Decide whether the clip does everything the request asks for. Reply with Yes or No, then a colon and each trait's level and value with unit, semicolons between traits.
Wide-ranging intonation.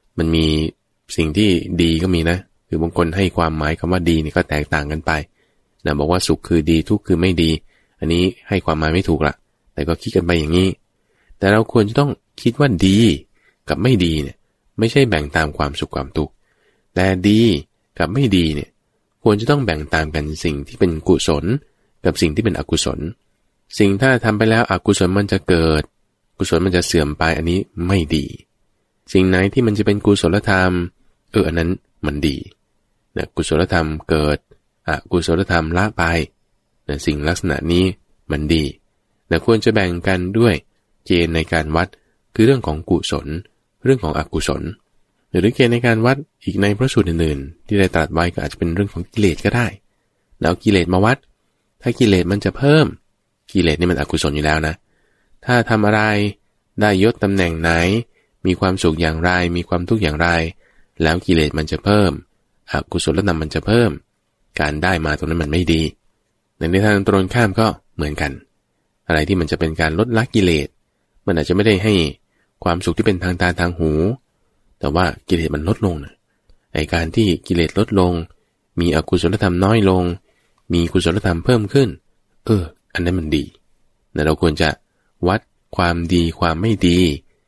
No: average, 4.3 semitones